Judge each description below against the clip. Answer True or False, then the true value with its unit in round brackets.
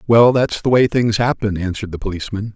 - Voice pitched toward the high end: False (105 Hz)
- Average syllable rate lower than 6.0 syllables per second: False (6.3 syllables/s)